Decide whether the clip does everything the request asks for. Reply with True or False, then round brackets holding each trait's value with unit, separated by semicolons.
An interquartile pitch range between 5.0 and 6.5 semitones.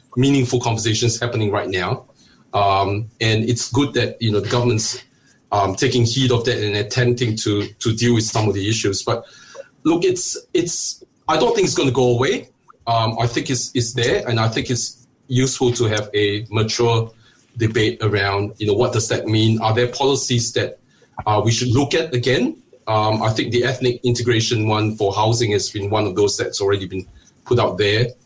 False (2.6 semitones)